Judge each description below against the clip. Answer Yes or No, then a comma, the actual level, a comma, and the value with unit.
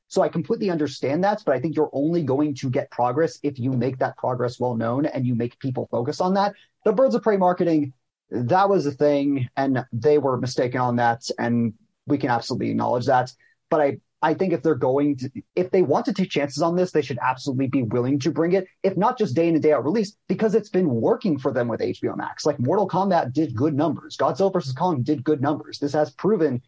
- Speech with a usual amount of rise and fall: No, wide, 5.7 semitones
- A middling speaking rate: No, fast, 240 wpm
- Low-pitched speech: No, medium, 150 Hz